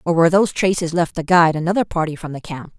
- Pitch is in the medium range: Yes, medium, 170 Hz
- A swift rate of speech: Yes, fast, 260 wpm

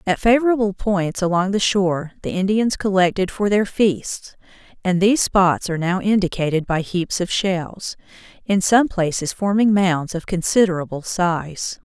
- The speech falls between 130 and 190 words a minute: Yes, average, 150 wpm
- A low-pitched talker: No, high, 190 Hz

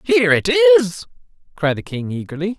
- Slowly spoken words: No, average, 160 wpm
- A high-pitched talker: Yes, high, 210 Hz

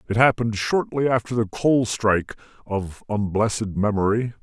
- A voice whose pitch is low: Yes, low, 110 Hz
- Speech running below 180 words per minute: Yes, slow, 135 wpm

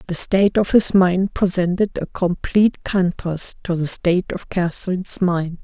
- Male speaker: No, female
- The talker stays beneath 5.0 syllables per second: Yes, 4.7 syllables/s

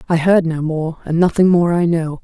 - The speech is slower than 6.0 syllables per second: Yes, 5.0 syllables/s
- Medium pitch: Yes, medium, 170 Hz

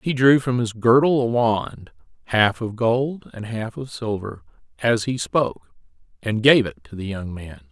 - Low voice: Yes, low, 115 Hz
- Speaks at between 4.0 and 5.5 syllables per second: Yes, 4.4 syllables/s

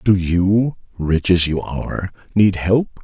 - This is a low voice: Yes, very low, 95 Hz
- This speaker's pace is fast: No, average, 160 wpm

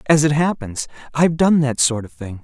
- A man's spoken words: Yes, male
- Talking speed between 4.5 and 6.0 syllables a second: Yes, 5.3 syllables/s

